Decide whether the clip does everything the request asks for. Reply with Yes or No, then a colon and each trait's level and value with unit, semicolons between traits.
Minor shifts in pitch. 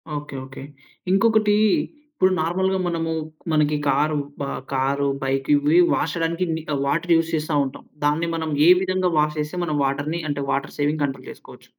No: average, 3.0 semitones